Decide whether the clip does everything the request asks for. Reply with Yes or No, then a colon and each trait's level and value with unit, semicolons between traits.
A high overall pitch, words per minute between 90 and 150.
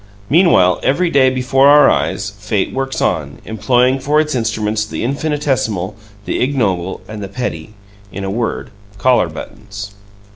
No: low, 115 Hz; average, 145 wpm